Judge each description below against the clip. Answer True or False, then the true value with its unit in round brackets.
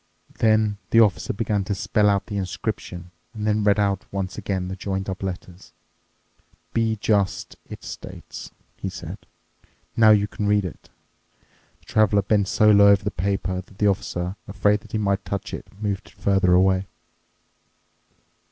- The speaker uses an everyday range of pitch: False (1.7 semitones)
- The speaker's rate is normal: True (165 wpm)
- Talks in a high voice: False (100 Hz)